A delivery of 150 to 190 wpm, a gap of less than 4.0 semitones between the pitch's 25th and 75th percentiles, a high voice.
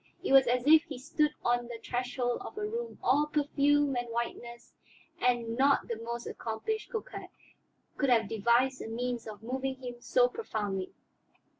Yes: average, 165 wpm; average, 3.6 semitones; very high, 250 Hz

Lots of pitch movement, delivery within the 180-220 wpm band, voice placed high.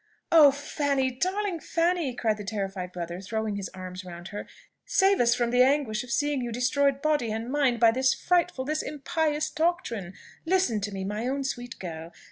Yes: wide, 6.2 semitones; average, 185 wpm; very high, 250 Hz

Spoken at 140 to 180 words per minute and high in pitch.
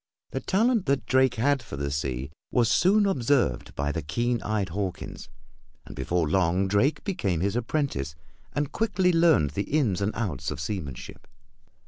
No: average, 160 wpm; low, 105 Hz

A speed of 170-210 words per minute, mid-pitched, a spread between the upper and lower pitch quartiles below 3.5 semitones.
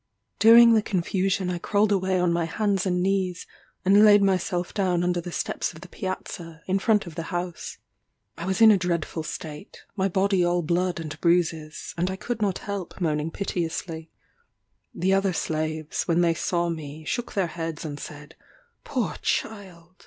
Yes: average, 175 wpm; medium, 180 Hz; average, 2.8 semitones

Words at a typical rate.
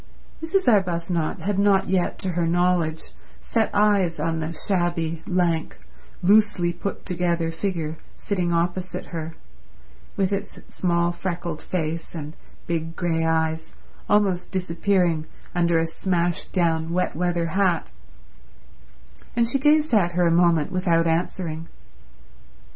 No: slow, 125 wpm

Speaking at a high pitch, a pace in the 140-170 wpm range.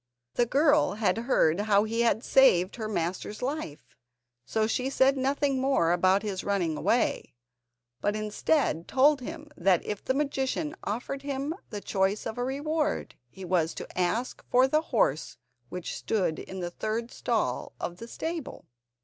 Yes: high, 225 Hz; average, 160 wpm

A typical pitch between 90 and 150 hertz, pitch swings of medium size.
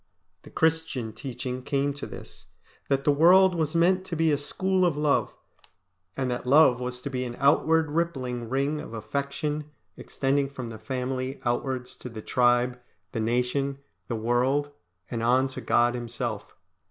Yes: low, 135 Hz; average, 3.2 semitones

